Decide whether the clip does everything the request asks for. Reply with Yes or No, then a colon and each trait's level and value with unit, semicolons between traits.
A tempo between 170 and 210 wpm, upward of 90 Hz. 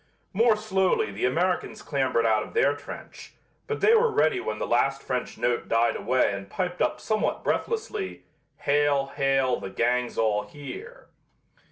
No: average, 160 wpm; medium, 140 Hz